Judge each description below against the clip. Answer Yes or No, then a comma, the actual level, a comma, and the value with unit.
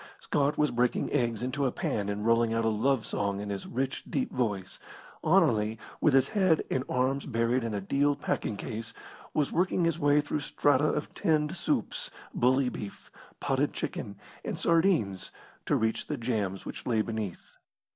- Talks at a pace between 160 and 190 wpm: Yes, average, 175 wpm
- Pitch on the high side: No, low, 125 Hz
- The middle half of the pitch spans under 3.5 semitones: No, average, 4.9 semitones